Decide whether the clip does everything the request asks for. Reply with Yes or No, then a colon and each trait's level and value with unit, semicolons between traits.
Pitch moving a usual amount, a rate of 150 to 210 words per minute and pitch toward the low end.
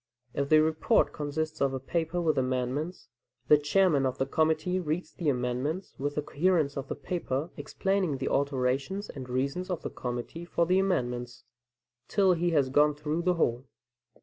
No: average, 4.5 semitones; average, 175 wpm; medium, 150 Hz